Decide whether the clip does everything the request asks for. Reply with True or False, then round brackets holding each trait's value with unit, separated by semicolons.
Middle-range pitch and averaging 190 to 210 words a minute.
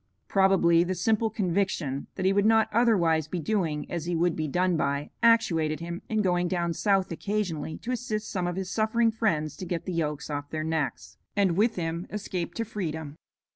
True (180 Hz; 195 wpm)